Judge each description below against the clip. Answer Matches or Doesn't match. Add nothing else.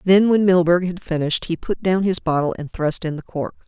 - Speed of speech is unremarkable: Doesn't match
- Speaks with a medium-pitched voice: Matches